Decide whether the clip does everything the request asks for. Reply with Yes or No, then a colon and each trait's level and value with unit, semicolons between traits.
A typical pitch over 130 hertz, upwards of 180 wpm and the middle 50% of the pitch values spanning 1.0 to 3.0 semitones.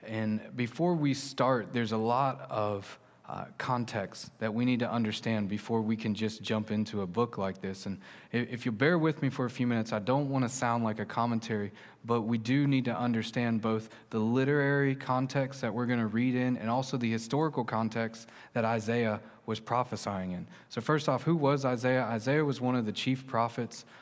No: low, 120 Hz; fast, 205 wpm; average, 2.7 semitones